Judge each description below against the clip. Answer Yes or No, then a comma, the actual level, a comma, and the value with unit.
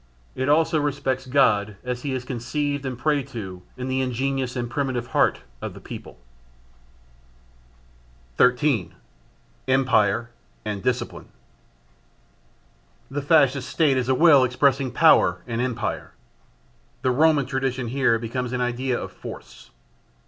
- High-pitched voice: No, low, 130 Hz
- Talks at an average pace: No, slow, 125 wpm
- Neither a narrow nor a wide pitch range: No, narrow, 2.2 semitones